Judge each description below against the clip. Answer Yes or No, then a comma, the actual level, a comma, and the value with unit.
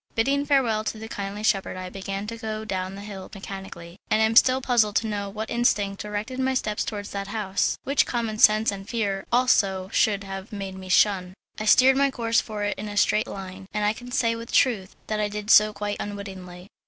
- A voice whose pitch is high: Yes, high, 210 Hz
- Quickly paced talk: Yes, fast, 220 wpm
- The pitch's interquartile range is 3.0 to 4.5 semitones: No, narrow, 2.5 semitones